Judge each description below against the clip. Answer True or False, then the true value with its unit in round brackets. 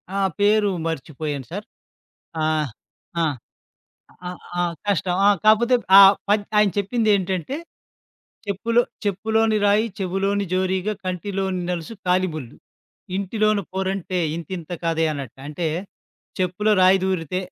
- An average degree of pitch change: True (3.0 semitones)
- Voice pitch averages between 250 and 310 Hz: False (190 Hz)